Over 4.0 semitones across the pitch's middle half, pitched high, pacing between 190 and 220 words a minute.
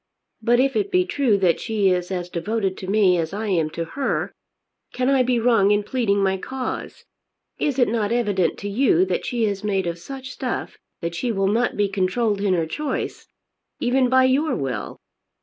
Yes: average, 5.1 semitones; high, 205 Hz; average, 200 wpm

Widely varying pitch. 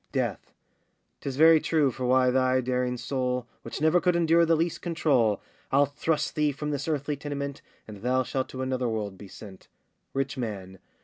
No: average, 3.2 semitones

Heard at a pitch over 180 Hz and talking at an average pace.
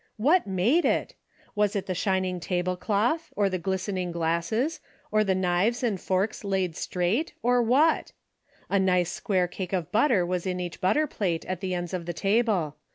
Yes: high, 190 Hz; average, 180 wpm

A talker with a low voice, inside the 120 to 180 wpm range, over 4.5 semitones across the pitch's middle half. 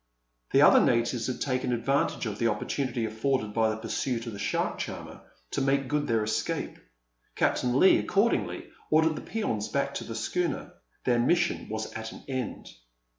No: low, 125 Hz; average, 175 wpm; average, 3.8 semitones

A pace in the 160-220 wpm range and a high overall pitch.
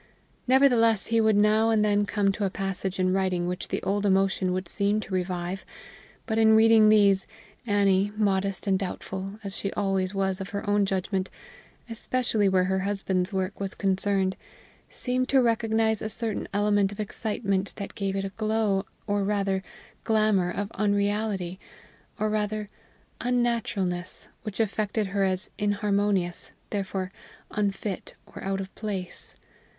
No: average, 150 wpm; high, 200 Hz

